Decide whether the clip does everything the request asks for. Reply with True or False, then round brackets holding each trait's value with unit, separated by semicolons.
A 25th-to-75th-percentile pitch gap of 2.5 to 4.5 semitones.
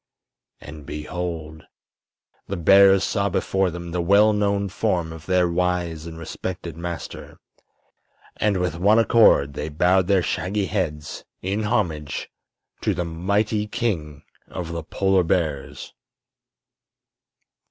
True (3.5 semitones)